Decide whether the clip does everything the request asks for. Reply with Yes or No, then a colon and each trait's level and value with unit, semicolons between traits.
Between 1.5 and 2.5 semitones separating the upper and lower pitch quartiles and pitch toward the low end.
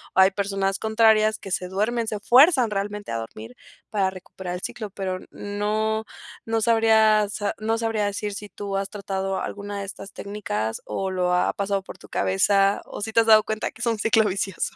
No: narrow, 2.1 semitones; high, 205 Hz